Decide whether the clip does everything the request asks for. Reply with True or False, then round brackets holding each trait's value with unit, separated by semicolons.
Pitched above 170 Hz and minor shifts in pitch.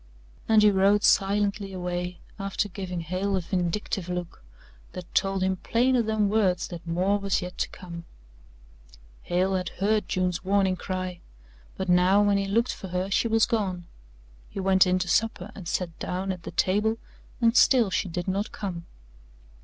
True (190 Hz; 2.2 semitones)